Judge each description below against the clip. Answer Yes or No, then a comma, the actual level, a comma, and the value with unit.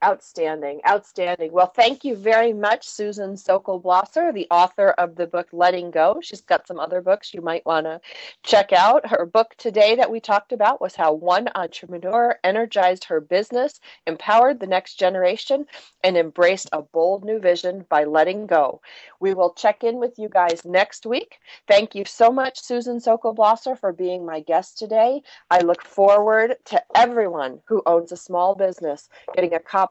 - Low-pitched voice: No, high, 195 Hz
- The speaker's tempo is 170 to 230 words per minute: Yes, average, 180 wpm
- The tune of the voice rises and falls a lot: No, average, 4.4 semitones